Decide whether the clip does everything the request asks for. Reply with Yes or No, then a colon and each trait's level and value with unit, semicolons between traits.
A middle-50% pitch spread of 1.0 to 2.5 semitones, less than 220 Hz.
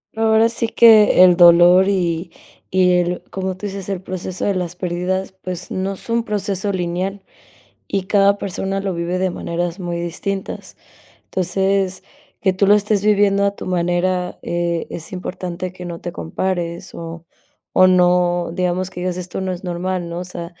Yes: narrow, 1.9 semitones; medium, 185 Hz